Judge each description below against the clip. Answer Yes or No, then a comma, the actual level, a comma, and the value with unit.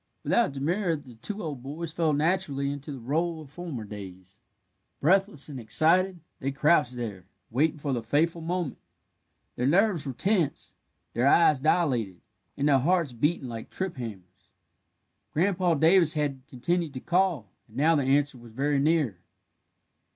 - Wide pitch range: No, average, 5.0 semitones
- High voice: No, medium, 145 Hz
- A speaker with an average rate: Yes, average, 155 wpm